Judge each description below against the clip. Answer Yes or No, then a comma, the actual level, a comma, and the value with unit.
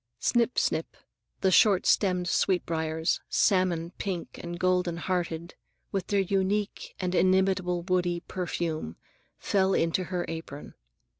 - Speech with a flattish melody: Yes, narrow, 1.9 semitones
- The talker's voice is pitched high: No, medium, 180 Hz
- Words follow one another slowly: Yes, slow, 125 wpm